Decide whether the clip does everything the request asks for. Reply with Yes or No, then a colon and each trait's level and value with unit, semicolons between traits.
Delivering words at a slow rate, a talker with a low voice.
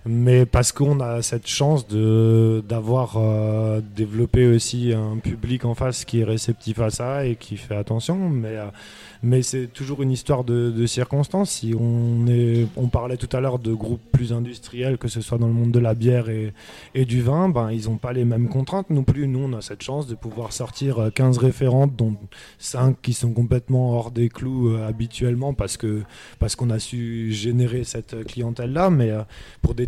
No: average, 205 wpm; low, 120 Hz